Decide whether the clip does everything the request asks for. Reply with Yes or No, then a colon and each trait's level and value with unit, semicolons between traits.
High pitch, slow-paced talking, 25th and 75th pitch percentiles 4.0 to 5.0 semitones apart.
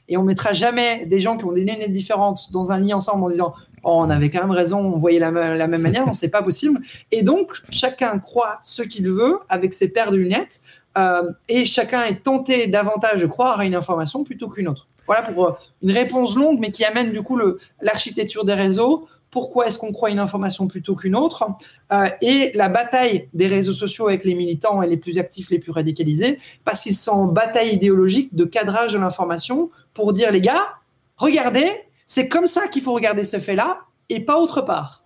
No: high, 205 Hz; average, 210 wpm; average, 4.6 semitones